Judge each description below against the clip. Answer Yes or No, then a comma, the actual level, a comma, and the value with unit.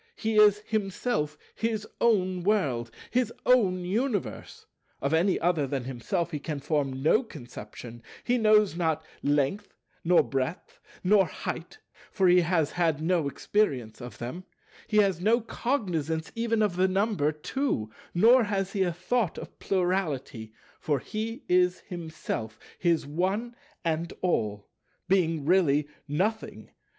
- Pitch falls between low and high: Yes, medium, 180 Hz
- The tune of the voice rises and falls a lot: Yes, wide, 5.9 semitones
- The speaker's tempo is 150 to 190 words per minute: No, average, 140 wpm